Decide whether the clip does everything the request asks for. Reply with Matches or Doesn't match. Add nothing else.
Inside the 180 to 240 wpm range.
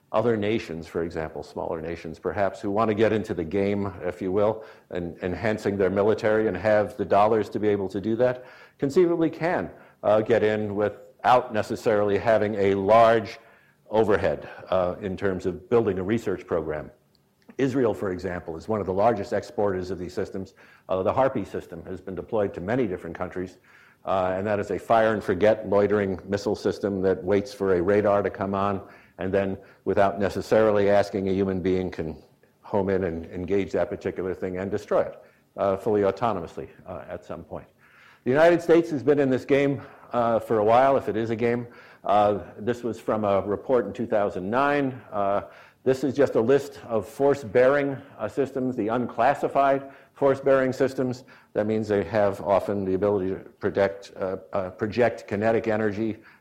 Matches